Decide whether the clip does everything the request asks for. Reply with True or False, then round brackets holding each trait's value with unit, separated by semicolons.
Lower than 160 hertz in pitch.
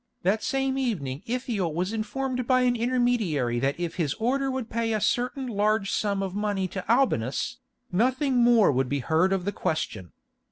False (215 Hz)